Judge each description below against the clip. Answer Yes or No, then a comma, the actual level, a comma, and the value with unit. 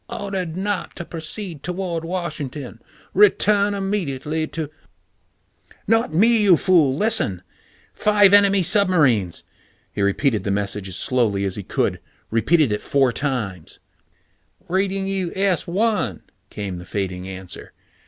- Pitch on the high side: No, medium, 160 Hz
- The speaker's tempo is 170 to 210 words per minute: No, average, 140 wpm